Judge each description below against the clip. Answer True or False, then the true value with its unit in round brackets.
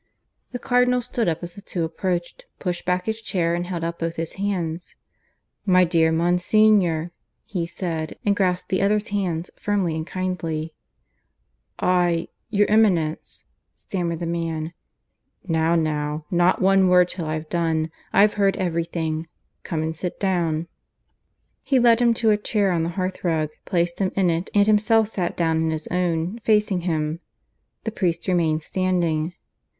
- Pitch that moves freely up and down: False (3.2 semitones)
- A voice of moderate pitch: True (175 Hz)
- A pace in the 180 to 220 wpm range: False (160 wpm)